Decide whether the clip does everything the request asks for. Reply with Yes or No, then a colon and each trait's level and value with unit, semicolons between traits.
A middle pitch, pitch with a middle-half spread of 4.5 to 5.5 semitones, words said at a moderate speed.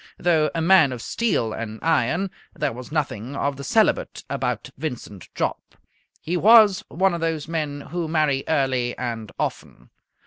Yes: medium, 150 Hz; average, 4.9 semitones; average, 160 wpm